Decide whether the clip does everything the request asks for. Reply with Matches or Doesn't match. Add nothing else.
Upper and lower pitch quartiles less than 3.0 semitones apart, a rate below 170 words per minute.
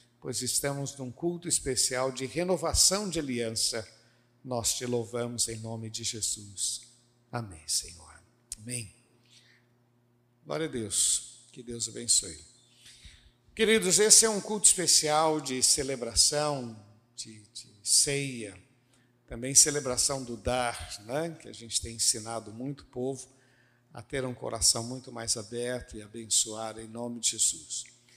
Matches